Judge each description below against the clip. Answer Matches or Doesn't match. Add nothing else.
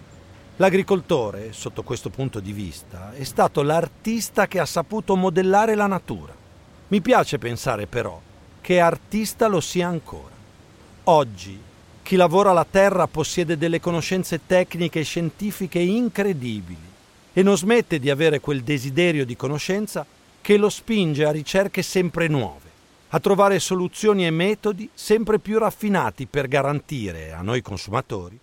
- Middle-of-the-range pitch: Matches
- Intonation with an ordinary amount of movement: Doesn't match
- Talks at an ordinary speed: Matches